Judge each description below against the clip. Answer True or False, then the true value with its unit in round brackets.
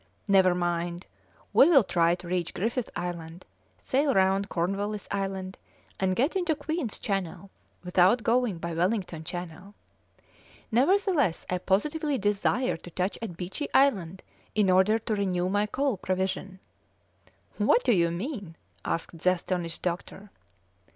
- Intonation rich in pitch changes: False (4.4 semitones)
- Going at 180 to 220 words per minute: False (135 wpm)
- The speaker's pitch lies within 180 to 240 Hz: True (190 Hz)